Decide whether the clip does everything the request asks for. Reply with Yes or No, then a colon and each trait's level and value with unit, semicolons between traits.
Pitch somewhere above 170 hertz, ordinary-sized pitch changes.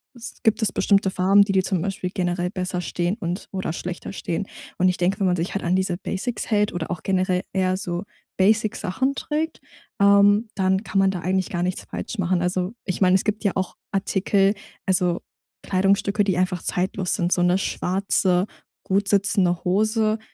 No: high, 190 Hz; narrow, 1.9 semitones